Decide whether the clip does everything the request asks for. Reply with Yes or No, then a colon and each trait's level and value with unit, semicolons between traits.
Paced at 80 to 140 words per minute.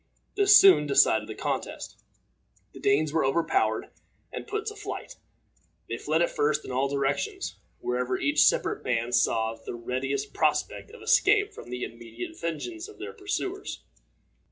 No: average, 155 wpm